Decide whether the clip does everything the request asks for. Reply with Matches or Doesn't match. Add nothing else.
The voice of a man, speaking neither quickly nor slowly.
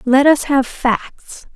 Doesn't match